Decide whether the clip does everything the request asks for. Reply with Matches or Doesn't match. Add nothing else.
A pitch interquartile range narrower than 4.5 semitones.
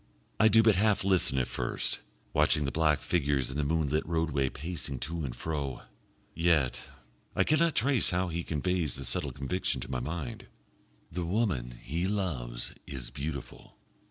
Doesn't match